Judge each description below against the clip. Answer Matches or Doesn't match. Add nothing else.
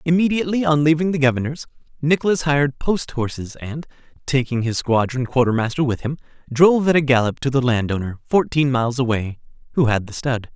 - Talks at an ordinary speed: Matches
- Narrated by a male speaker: Matches